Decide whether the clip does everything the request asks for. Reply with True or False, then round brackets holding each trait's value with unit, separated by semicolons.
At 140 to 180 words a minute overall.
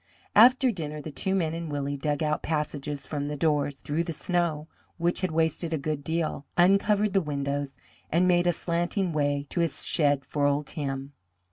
False (190 wpm)